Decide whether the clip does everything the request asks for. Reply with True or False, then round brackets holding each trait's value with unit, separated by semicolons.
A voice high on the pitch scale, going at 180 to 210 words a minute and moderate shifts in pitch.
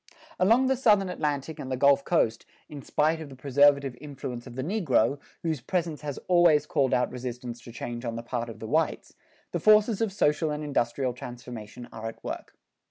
False (140 Hz; 195 wpm; 4.8 semitones)